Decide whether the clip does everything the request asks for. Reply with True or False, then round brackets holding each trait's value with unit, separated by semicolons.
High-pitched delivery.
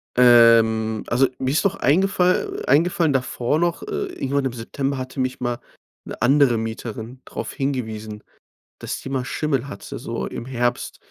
False (130 Hz)